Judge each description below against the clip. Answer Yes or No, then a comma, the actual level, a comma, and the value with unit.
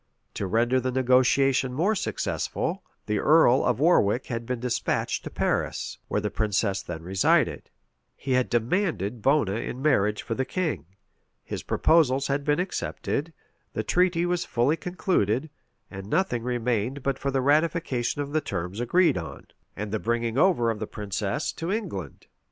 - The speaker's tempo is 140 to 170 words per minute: Yes, average, 155 wpm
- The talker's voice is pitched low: Yes, low, 125 Hz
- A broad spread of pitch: Yes, wide, 5.9 semitones